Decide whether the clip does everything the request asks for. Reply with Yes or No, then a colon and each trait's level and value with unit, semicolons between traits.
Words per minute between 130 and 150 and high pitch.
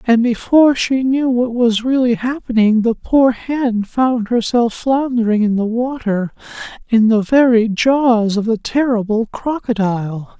Yes: average, 145 wpm; high, 235 Hz